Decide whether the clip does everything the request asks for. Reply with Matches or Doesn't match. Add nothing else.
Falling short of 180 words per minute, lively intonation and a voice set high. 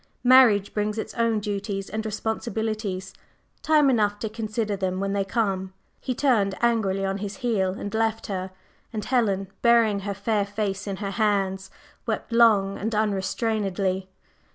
Doesn't match